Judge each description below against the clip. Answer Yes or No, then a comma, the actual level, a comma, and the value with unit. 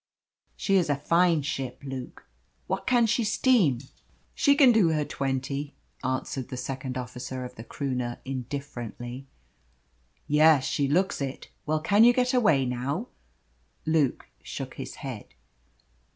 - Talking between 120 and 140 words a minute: Yes, slow, 135 wpm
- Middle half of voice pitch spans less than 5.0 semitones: No, wide, 5.6 semitones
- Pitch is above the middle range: No, medium, 140 Hz